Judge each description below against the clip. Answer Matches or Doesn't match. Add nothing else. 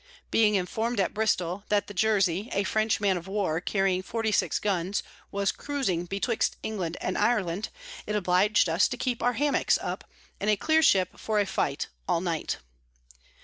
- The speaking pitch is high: Matches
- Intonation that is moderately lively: Matches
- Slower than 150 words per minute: Doesn't match